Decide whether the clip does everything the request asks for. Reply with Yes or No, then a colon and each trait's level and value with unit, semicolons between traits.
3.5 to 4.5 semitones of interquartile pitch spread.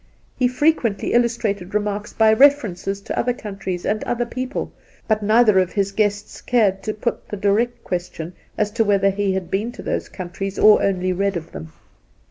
No: average, 3.1 semitones